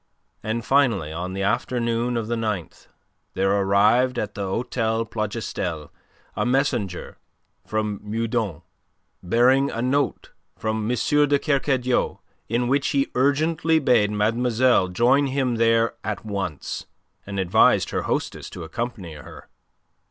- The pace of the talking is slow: Yes, slow, 130 wpm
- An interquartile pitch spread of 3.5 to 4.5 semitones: Yes, average, 3.9 semitones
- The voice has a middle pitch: No, low, 115 Hz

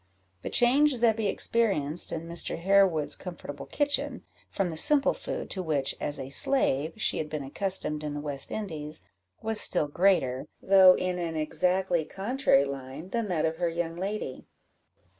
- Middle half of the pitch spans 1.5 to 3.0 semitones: No, average, 4.7 semitones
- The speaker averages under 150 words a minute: No, average, 160 wpm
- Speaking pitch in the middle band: Yes, medium, 170 Hz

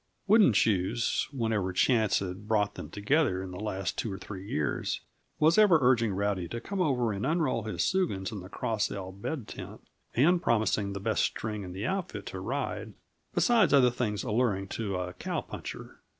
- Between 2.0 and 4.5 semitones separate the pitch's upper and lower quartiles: No, average, 5.1 semitones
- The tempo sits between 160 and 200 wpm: Yes, average, 185 wpm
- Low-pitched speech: Yes, low, 110 Hz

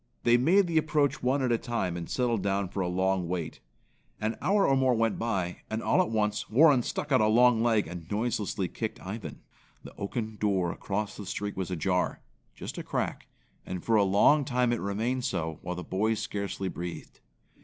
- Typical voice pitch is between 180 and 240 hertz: No, low, 110 Hz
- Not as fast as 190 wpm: No, average, 200 wpm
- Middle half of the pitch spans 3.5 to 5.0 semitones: Yes, average, 4.5 semitones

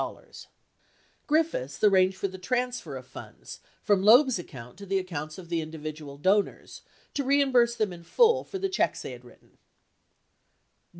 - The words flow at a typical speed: Yes, average, 160 wpm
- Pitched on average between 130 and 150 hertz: No, high, 190 Hz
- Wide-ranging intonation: Yes, wide, 7.9 semitones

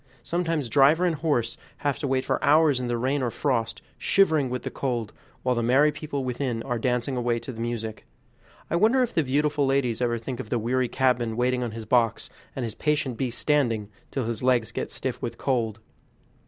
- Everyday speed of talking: No, fast, 210 wpm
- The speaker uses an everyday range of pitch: Yes, average, 3.5 semitones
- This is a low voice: Yes, low, 125 Hz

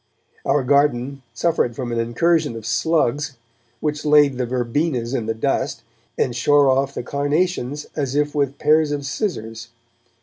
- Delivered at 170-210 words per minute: No, average, 155 wpm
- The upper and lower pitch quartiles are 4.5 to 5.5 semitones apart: No, average, 3.5 semitones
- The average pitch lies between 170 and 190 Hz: No, medium, 140 Hz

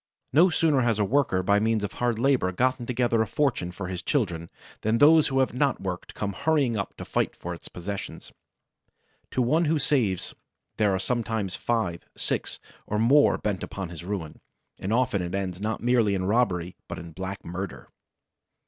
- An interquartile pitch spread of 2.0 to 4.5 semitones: No, average, 5.2 semitones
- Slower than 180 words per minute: No, average, 185 wpm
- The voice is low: Yes, low, 110 Hz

